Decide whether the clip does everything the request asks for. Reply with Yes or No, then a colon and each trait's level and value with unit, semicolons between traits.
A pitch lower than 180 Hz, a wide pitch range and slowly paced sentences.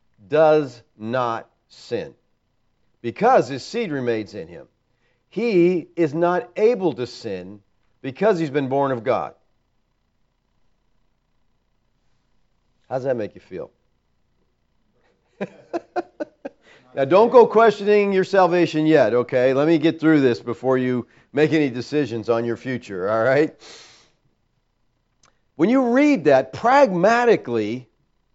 Yes: medium, 140 Hz; wide, 6.5 semitones; slow, 115 wpm